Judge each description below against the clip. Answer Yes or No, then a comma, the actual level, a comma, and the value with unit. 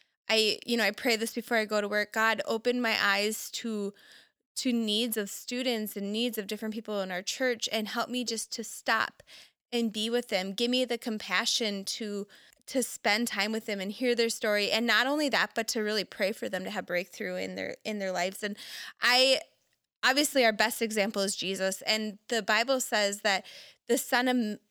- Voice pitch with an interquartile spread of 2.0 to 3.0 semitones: Yes, narrow, 2.6 semitones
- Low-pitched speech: No, high, 220 Hz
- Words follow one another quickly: Yes, fast, 210 wpm